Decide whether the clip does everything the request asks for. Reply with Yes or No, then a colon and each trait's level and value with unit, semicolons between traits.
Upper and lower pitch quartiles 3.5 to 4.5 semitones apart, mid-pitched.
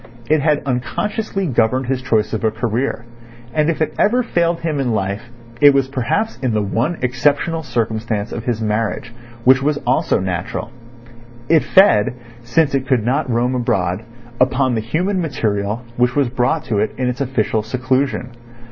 No: average, 4.1 semitones; low, 125 Hz